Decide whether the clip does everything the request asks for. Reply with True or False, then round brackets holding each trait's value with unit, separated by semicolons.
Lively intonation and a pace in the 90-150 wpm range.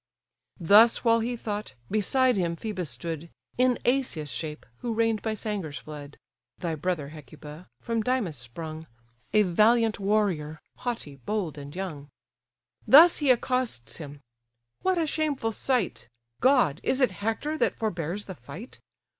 True (7.1 semitones; 140 wpm)